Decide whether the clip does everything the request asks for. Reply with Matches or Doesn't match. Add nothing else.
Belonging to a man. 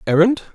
Matches